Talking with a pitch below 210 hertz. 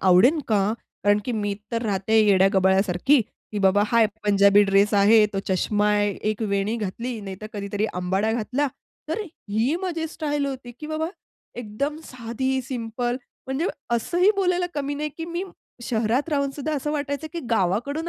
No: high, 230 Hz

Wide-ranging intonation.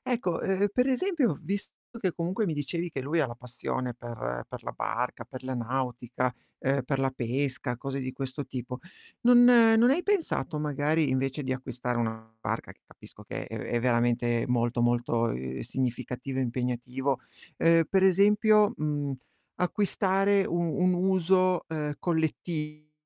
Yes: wide, 6.8 semitones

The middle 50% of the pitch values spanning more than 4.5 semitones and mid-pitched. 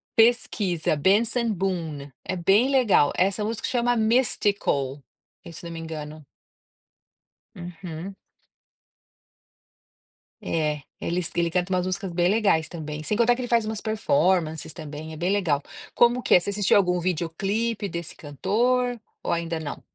Yes: average, 5.3 semitones; medium, 180 Hz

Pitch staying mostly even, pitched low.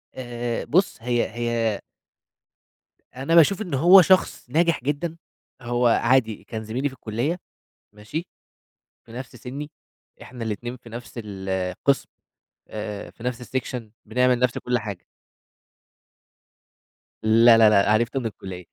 No: average, 3.3 semitones; low, 120 Hz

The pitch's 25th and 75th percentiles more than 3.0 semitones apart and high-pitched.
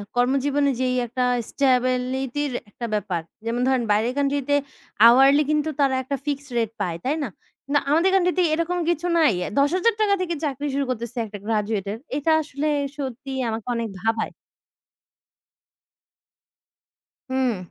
Yes: average, 3.7 semitones; very high, 265 Hz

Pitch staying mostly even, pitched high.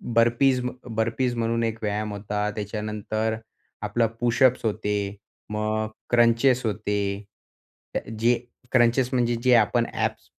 No: narrow, 2.1 semitones; low, 115 Hz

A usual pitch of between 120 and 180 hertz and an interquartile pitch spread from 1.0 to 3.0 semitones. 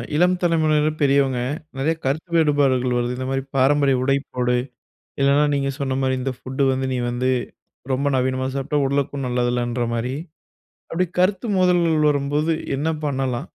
Yes: low, 135 Hz; narrow, 2.5 semitones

